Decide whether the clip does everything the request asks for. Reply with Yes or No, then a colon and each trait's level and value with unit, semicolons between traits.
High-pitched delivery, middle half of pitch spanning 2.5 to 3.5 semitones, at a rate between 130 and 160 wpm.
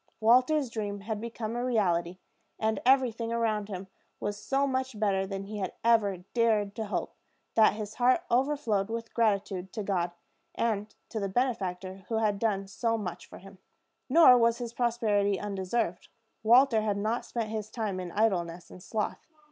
No: high, 215 Hz; average, 2.9 semitones; average, 170 wpm